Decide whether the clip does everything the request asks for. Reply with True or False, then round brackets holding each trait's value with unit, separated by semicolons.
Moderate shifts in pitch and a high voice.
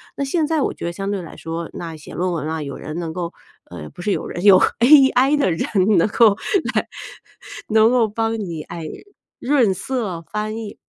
False (5.7 semitones; 200 Hz)